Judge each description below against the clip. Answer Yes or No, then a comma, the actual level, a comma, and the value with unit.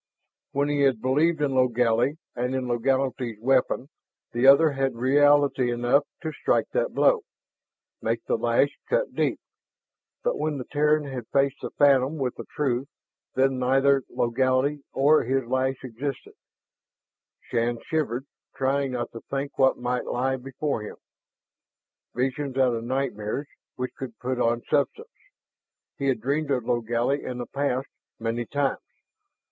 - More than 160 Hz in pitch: No, low, 130 Hz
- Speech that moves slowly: No, average, 150 wpm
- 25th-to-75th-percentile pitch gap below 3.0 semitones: Yes, narrow, 2.5 semitones